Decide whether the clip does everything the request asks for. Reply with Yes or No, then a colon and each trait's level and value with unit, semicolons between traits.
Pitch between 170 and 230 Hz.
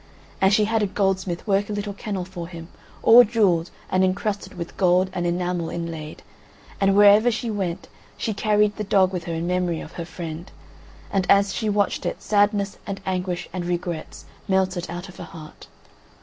Yes: high, 190 Hz